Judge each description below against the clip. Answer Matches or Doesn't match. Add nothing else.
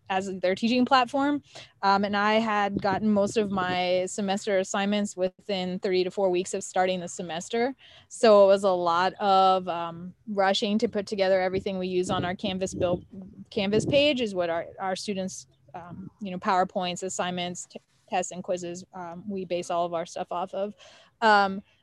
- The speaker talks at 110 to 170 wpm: Doesn't match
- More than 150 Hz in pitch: Matches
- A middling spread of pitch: Doesn't match